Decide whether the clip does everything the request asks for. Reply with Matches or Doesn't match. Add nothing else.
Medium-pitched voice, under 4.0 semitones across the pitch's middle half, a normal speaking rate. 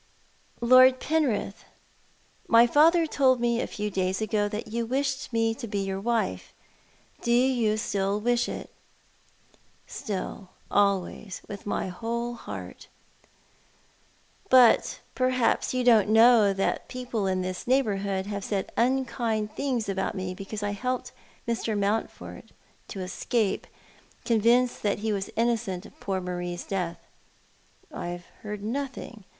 Doesn't match